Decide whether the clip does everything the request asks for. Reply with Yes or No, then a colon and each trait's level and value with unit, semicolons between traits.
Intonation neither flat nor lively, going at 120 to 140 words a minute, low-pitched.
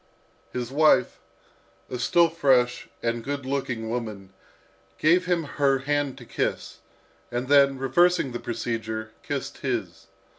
Yes: average, 3.3 semitones; slow, 135 wpm; low, 130 Hz